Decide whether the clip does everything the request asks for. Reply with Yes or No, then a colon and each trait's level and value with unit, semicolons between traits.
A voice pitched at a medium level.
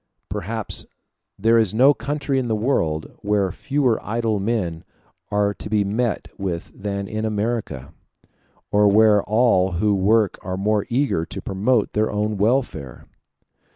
No: low, 105 Hz